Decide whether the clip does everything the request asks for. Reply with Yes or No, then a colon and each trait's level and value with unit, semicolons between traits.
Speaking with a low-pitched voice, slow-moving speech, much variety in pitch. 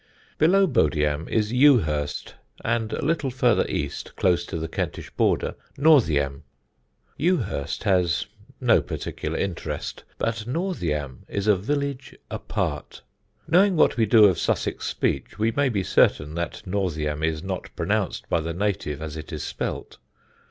No: low, 100 Hz; average, 145 wpm; wide, 8.1 semitones